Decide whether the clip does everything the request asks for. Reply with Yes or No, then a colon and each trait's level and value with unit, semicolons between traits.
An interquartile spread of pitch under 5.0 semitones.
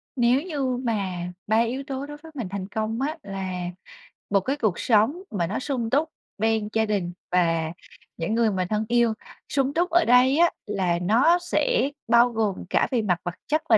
No: average, 5.3 semitones